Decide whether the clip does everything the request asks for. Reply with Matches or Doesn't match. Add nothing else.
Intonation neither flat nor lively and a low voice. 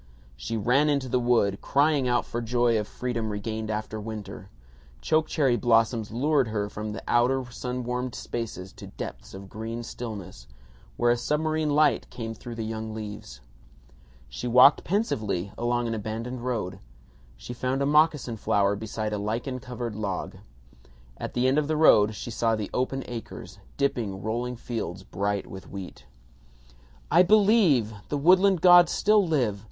Matches